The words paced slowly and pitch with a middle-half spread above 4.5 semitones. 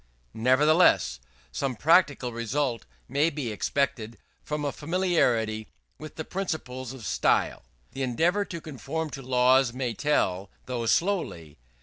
Yes: slow, 125 wpm; average, 5.1 semitones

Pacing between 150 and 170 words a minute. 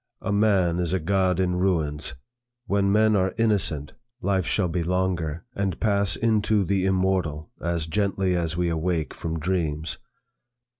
Yes: average, 155 wpm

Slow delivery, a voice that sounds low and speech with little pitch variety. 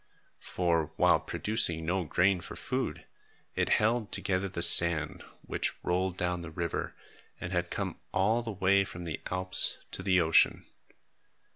No: average, 150 wpm; very low, 90 Hz; narrow, 2.2 semitones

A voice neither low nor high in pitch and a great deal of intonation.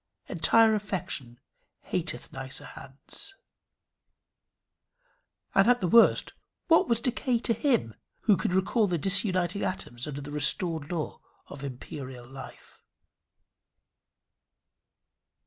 Yes: medium, 180 Hz; wide, 7.8 semitones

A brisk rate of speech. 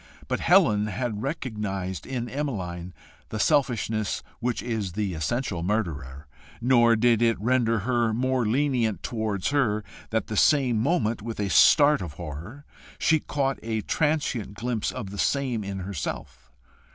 No: average, 145 wpm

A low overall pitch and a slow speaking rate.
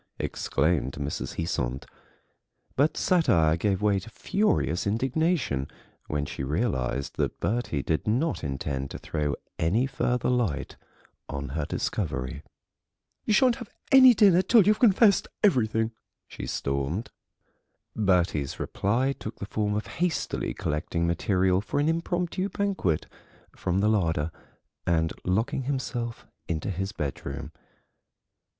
Yes: low, 100 Hz; slow, 125 wpm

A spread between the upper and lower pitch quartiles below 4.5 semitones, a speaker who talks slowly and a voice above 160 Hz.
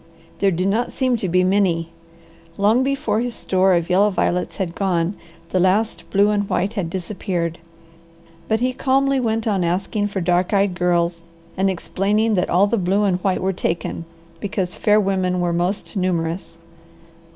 No: average, 2.8 semitones; average, 170 wpm; high, 190 Hz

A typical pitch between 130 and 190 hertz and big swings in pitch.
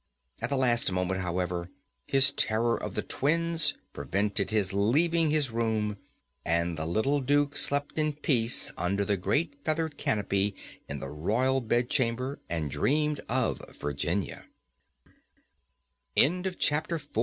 No: low, 115 Hz; wide, 6.6 semitones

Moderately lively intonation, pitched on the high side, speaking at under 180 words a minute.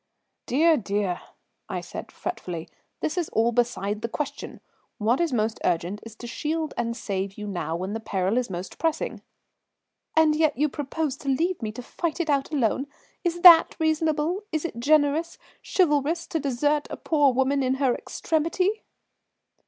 No: wide, 6.1 semitones; very high, 275 Hz; average, 170 wpm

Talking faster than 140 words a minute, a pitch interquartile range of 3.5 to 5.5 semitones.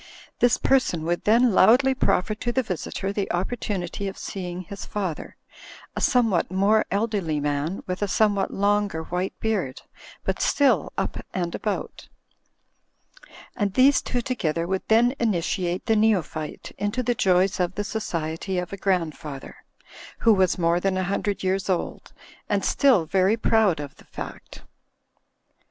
Yes: average, 150 wpm; average, 3.8 semitones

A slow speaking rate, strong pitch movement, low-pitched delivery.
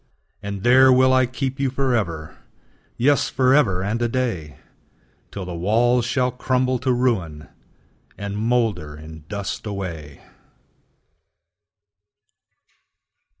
Yes: slow, 105 wpm; wide, 5.8 semitones; low, 115 Hz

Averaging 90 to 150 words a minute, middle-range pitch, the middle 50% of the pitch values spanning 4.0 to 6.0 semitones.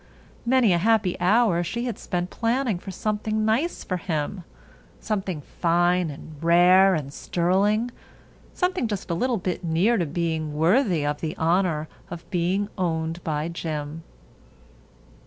Yes: average, 140 wpm; medium, 180 Hz; average, 4.5 semitones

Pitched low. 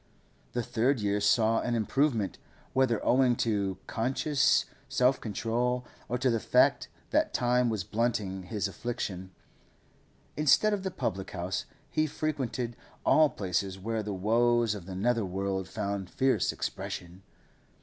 Yes: low, 115 Hz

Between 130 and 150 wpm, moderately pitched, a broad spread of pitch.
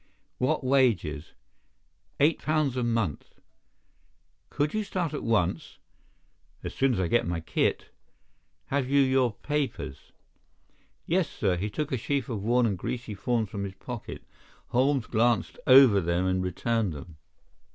No: average, 145 wpm; low, 120 Hz; wide, 6.1 semitones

